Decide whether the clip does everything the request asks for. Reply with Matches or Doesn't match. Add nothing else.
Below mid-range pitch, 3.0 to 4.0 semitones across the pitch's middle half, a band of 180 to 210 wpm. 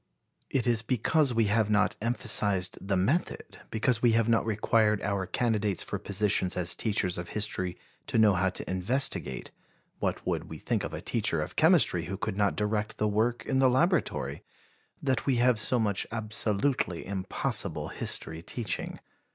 Doesn't match